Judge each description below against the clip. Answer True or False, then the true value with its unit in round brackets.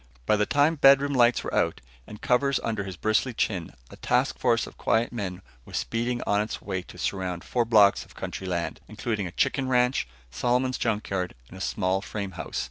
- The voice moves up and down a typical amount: True (4.6 semitones)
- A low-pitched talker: True (110 Hz)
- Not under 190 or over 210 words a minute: True (205 wpm)